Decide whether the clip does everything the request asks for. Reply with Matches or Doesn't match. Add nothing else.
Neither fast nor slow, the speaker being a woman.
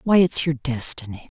Matches